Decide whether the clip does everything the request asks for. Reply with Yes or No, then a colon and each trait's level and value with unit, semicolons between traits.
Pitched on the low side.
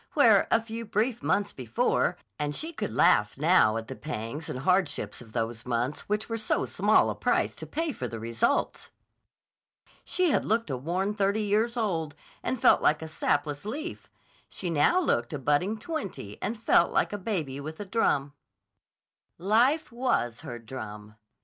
No: medium, 170 Hz